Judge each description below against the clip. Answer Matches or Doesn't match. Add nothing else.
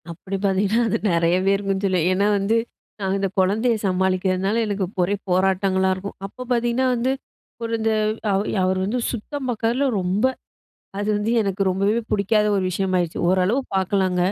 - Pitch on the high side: Matches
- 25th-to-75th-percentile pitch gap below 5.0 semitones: Matches